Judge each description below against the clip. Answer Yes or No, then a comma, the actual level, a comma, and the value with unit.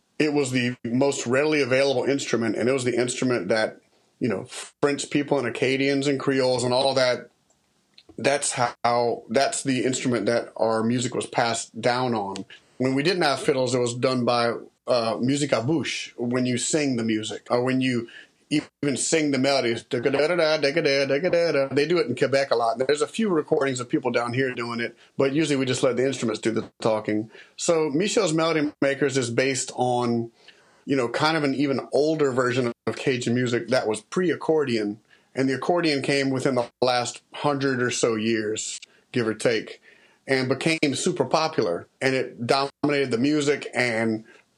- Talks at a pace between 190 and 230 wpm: No, average, 180 wpm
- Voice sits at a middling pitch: No, low, 130 Hz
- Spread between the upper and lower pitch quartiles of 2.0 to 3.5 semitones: Yes, average, 3.0 semitones